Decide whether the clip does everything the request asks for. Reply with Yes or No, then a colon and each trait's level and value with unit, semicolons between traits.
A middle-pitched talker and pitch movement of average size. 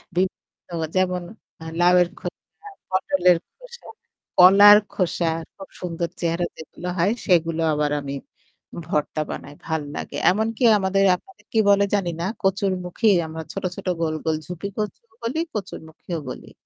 Yes: medium, 180 Hz; average, 3.1 semitones